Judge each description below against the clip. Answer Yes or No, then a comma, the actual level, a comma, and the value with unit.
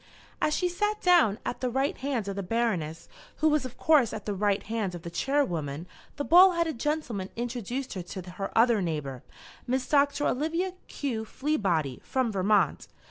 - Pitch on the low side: No, high, 235 Hz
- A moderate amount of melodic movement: No, wide, 7.1 semitones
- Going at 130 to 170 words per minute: No, average, 180 wpm